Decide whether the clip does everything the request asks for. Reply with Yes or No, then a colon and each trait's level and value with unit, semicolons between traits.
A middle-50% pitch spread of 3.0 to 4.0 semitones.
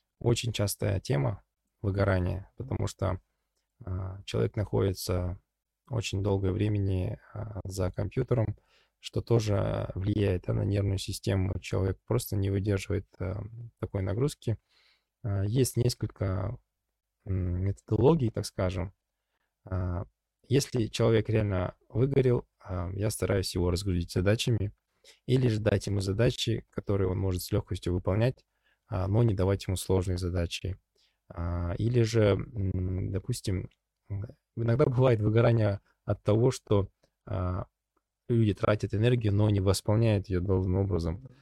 Yes: average, 3.3 semitones